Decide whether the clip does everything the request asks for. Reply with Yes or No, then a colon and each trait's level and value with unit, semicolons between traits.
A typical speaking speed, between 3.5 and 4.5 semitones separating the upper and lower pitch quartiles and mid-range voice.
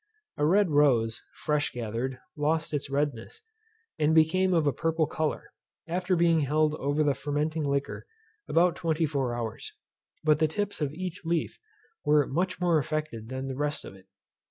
No: average, 165 wpm; average, 2.7 semitones; medium, 150 Hz